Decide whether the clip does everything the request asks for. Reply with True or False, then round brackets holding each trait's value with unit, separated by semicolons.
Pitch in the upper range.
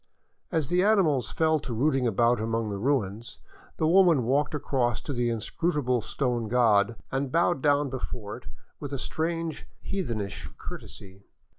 False (130 Hz)